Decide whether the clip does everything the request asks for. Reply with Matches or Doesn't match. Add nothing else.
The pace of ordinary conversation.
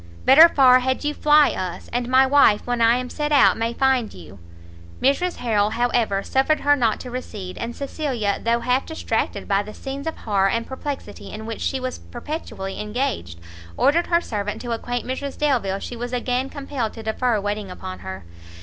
Matches